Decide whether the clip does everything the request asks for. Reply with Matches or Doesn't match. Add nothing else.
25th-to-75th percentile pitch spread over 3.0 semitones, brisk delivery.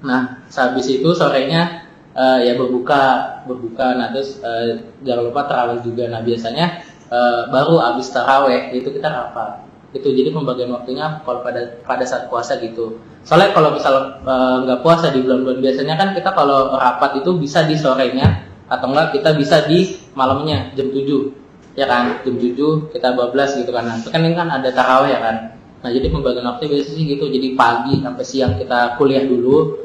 Doesn't match